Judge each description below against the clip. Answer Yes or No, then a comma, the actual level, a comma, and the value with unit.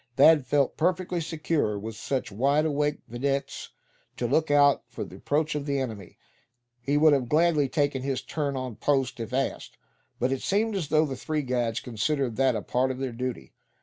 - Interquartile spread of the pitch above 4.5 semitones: No, average, 3.2 semitones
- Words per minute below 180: No, average, 190 wpm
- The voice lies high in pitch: No, medium, 140 Hz